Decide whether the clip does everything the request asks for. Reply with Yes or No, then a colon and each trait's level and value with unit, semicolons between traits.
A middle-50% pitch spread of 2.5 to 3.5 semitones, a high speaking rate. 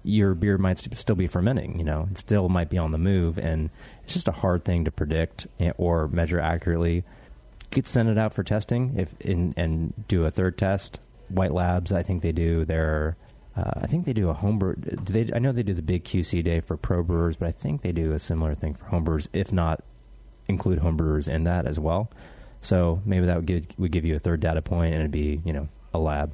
Yes: average, 3.2 semitones; fast, 230 wpm